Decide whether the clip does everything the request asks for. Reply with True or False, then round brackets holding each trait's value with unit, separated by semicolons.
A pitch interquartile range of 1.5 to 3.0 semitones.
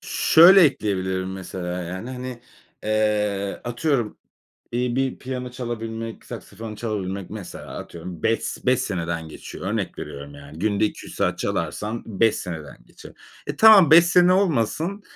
False (5.2 semitones)